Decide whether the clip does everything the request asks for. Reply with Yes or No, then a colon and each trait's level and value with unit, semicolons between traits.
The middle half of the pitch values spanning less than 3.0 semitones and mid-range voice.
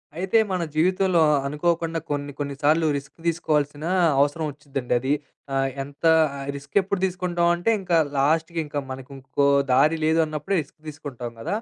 No: average, 3.3 semitones; medium, 155 Hz